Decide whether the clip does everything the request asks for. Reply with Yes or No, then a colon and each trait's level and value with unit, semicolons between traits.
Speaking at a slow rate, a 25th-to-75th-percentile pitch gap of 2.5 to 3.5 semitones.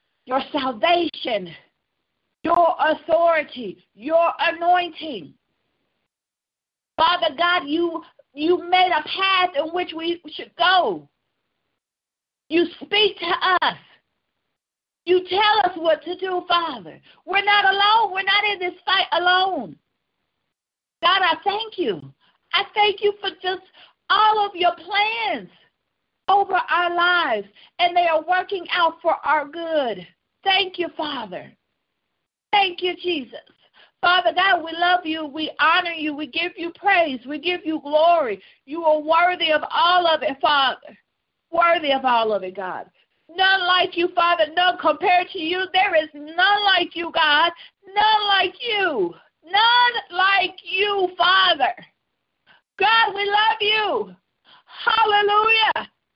Yes: slow, 130 wpm; average, 3.1 semitones